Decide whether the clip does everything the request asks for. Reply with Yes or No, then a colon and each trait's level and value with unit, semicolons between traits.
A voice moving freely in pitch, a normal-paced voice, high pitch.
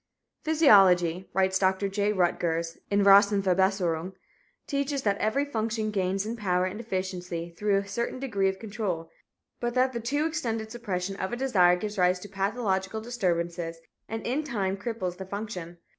No: average, 3.7 semitones; average, 160 wpm; high, 200 Hz